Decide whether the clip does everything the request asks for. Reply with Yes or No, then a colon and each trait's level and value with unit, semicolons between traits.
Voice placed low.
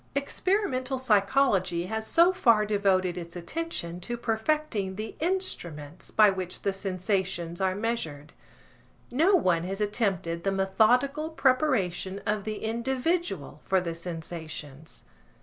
No: high, 200 Hz